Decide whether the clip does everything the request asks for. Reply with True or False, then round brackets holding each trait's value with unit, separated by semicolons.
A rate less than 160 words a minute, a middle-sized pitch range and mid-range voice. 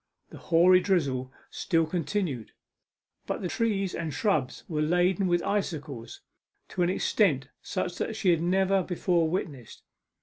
True (140 wpm; 3.9 semitones; 175 Hz)